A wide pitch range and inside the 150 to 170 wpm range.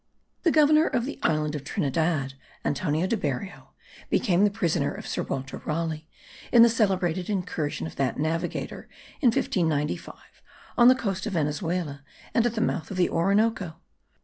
Yes: wide, 5.9 semitones; average, 160 wpm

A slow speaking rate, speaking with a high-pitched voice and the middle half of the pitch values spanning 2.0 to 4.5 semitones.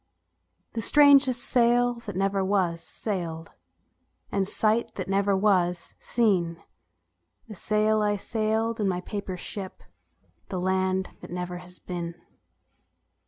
Yes: slow, 120 wpm; high, 195 Hz; average, 3.3 semitones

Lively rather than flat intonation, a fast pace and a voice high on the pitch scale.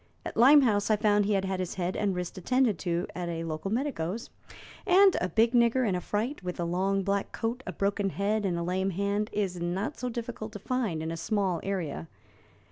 No: average, 3.9 semitones; fast, 215 wpm; high, 200 Hz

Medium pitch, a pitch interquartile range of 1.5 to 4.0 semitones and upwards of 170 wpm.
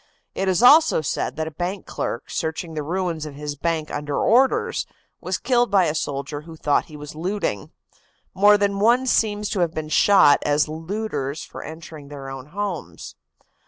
No: medium, 160 Hz; average, 5.3 semitones; average, 180 wpm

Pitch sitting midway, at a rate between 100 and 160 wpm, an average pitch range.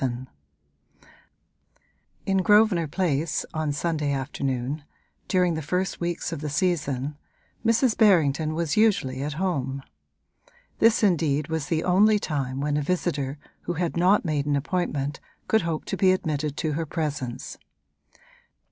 Yes: medium, 155 Hz; average, 140 wpm; average, 4.1 semitones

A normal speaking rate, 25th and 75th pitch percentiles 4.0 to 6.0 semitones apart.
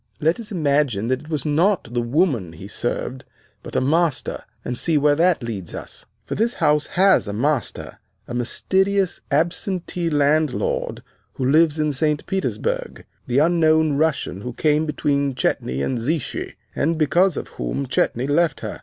Yes: average, 165 wpm; average, 4.6 semitones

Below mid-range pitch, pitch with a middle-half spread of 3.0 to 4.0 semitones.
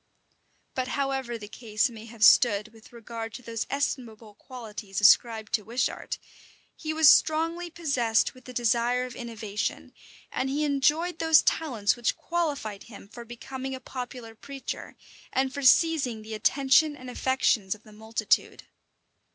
No: high, 245 Hz; average, 3.7 semitones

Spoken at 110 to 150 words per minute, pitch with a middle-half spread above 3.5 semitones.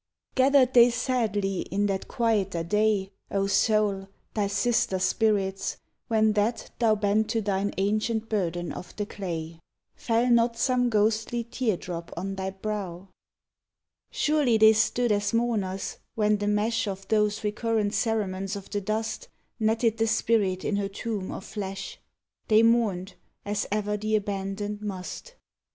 No: average, 145 wpm; narrow, 2.6 semitones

